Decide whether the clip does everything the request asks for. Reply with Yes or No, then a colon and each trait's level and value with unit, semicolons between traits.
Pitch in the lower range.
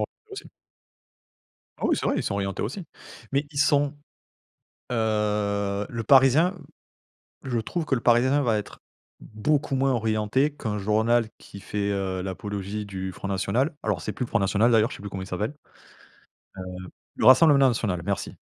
Yes: low, 110 Hz